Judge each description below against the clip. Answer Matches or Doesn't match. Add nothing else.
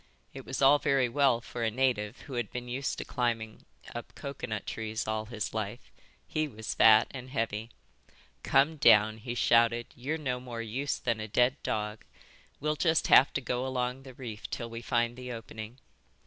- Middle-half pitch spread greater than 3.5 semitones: Doesn't match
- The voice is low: Matches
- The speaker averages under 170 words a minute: Doesn't match